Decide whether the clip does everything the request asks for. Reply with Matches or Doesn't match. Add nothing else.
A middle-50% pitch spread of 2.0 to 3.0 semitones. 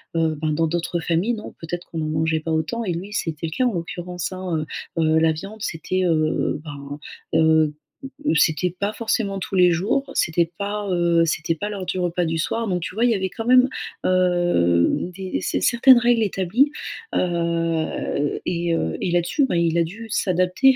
Doesn't match